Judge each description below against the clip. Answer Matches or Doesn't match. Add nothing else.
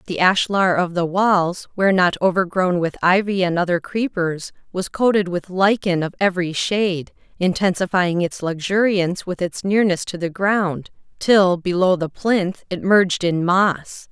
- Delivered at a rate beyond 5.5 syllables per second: Doesn't match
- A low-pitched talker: Doesn't match